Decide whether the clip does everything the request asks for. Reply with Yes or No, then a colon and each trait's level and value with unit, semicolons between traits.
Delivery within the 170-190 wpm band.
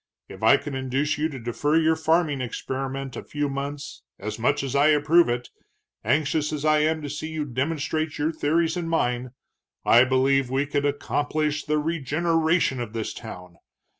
Yes: average, 175 wpm